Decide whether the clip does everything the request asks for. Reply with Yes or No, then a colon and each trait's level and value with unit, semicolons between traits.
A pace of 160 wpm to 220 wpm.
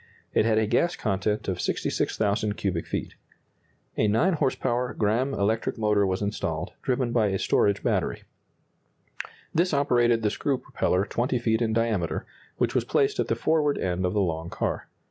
Yes: average, 170 wpm